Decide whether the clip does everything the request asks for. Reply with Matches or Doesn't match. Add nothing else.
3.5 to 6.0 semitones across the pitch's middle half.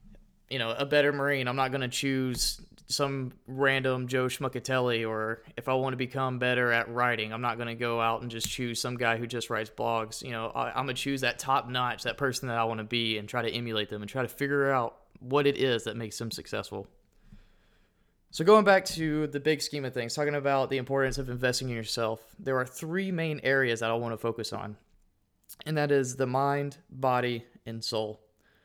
Doesn't match